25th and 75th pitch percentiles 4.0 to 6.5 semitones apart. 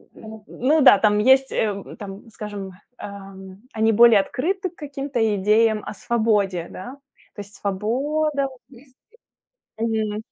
Yes: average, 4.5 semitones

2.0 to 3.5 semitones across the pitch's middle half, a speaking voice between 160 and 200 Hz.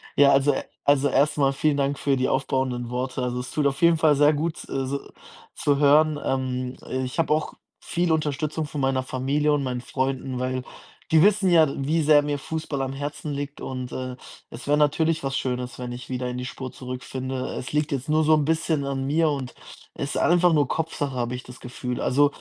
No: average, 2.8 semitones; medium, 140 Hz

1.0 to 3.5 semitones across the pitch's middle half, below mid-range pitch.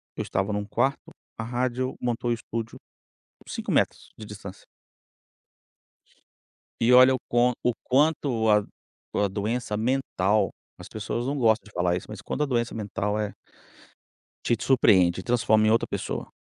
Yes: average, 3.1 semitones; low, 115 Hz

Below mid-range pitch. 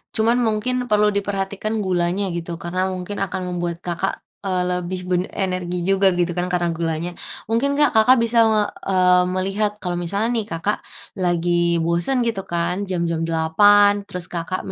No: medium, 185 Hz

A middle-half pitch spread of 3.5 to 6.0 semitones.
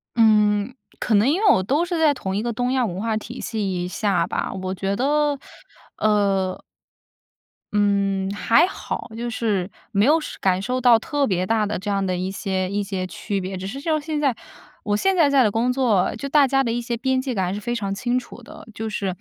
Yes: average, 4.7 semitones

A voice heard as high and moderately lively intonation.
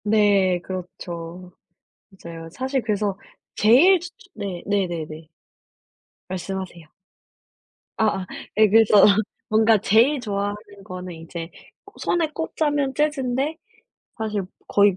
Yes: high, 205 Hz; average, 5.0 semitones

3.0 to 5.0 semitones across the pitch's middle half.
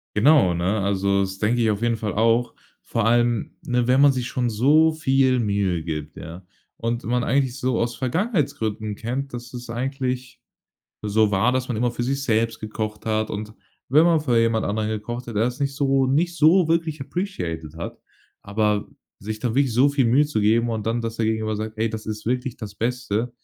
Yes: average, 3.4 semitones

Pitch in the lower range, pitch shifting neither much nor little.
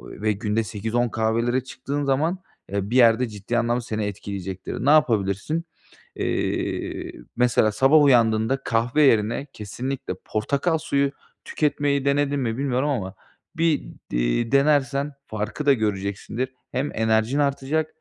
Yes: low, 120 Hz; average, 4.4 semitones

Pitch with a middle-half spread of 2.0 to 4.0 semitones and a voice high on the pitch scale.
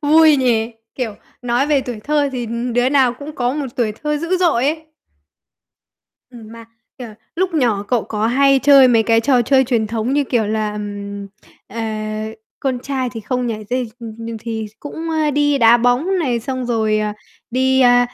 Yes: average, 3.6 semitones; high, 245 Hz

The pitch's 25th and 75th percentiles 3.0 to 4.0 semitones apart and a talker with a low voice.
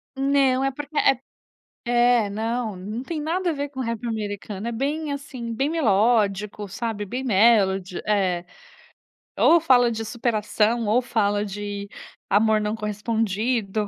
No: average, 3.7 semitones; high, 225 Hz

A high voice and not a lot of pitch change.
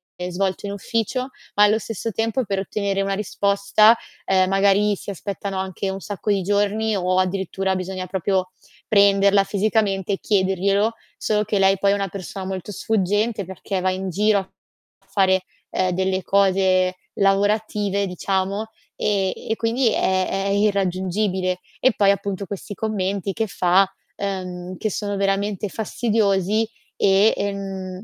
Yes: high, 195 Hz; narrow, 1.6 semitones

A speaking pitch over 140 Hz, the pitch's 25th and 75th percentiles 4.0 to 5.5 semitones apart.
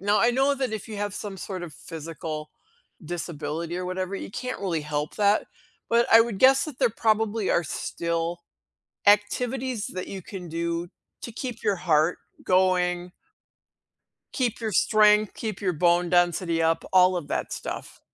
Yes: medium, 185 Hz; average, 4.3 semitones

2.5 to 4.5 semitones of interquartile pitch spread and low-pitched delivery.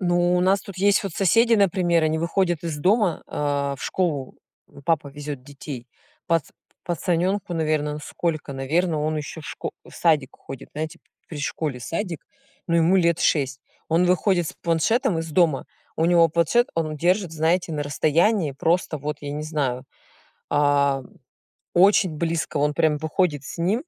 No: average, 3.2 semitones; medium, 165 Hz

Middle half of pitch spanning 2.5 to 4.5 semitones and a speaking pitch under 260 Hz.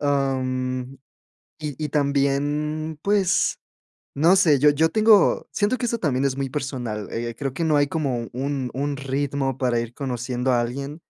Yes: average, 2.9 semitones; medium, 140 Hz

